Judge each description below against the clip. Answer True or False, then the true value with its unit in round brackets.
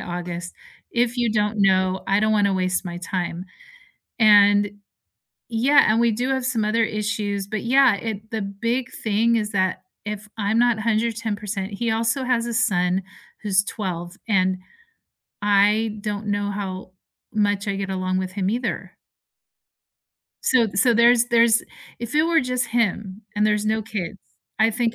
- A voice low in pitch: False (210 Hz)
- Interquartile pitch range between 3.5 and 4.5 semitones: False (2.8 semitones)